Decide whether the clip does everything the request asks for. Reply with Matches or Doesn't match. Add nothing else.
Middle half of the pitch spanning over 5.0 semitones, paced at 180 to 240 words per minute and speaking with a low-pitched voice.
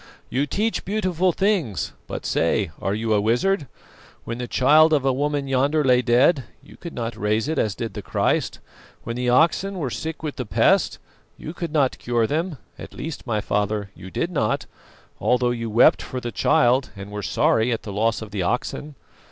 Matches